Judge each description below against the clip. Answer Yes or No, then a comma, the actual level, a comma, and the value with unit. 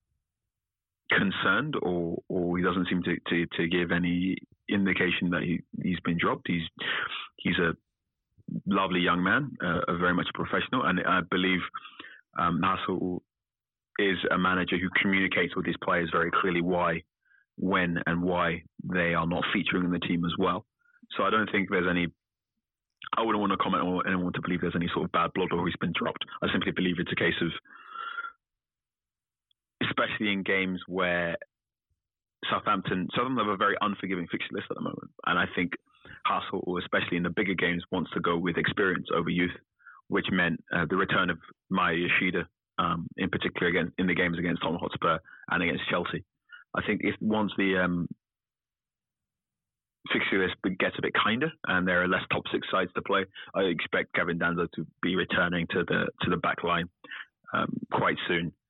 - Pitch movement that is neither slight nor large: No, narrow, 1.6 semitones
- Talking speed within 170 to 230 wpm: Yes, average, 180 wpm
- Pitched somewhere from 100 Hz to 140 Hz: No, very low, 90 Hz